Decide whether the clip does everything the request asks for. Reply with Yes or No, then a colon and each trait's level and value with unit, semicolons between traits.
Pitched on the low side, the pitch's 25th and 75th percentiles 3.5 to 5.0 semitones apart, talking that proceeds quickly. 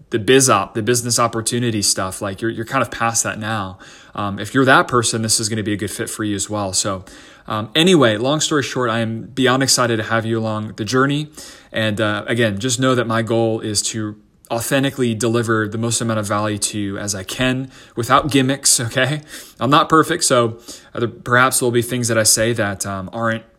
No: low, 115 Hz; average, 3.0 semitones; fast, 220 wpm